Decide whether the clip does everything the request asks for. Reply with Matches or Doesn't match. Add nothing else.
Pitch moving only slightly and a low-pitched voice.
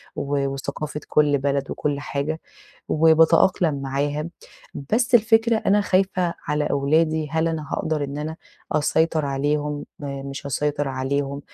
Doesn't match